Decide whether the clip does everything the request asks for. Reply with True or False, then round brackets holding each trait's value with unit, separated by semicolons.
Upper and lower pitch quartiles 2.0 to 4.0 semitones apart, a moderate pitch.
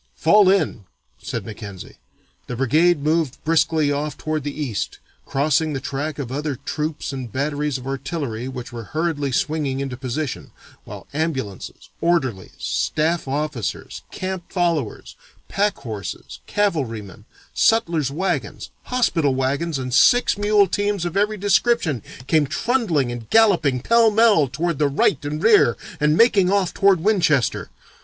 False (5.0 semitones; 150 Hz)